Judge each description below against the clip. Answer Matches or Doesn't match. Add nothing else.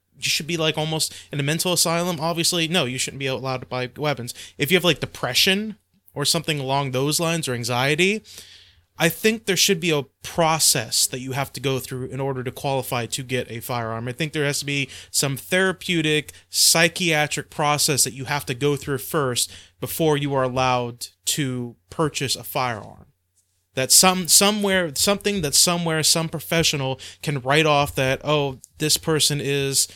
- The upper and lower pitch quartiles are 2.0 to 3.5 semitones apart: Doesn't match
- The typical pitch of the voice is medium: Matches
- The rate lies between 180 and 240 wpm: Matches